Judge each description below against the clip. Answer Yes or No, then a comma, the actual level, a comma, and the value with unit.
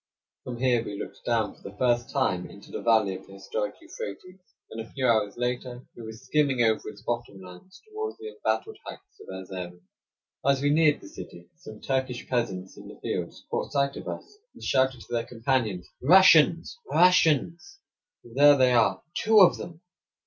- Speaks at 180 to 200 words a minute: Yes, average, 185 wpm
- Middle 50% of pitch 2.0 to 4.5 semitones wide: No, wide, 5.6 semitones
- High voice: No, low, 125 Hz